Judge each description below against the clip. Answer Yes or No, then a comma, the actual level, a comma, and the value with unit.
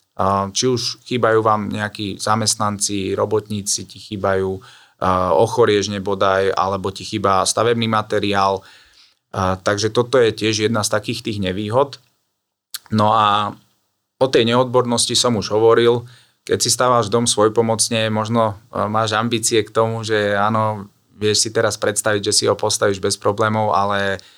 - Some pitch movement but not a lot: No, narrow, 2.1 semitones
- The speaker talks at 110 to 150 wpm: Yes, average, 140 wpm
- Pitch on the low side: Yes, low, 105 Hz